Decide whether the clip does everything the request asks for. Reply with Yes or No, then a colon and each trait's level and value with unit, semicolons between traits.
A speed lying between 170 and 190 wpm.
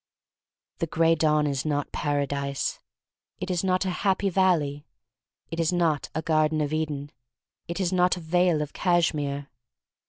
No: average, 155 wpm